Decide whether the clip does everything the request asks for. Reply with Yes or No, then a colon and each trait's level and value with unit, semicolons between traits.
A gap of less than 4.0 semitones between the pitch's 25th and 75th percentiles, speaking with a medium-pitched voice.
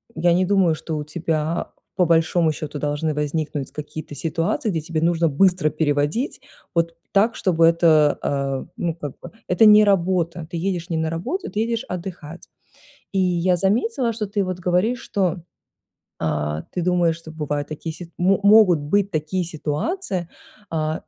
Yes: average, 3.3 semitones; medium, 170 Hz